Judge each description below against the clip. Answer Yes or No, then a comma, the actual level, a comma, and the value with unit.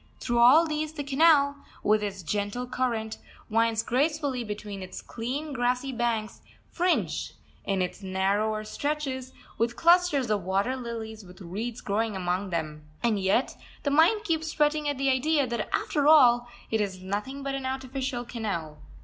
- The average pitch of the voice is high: Yes, high, 240 Hz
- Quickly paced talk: No, average, 160 wpm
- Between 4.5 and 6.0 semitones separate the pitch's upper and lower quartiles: Yes, average, 5.2 semitones